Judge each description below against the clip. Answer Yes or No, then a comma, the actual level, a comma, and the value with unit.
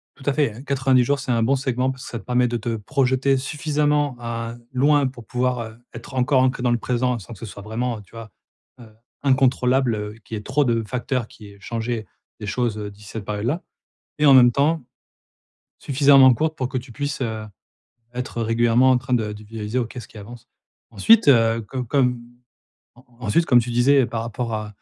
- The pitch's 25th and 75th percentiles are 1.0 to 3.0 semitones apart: Yes, narrow, 2.6 semitones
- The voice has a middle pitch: No, low, 125 Hz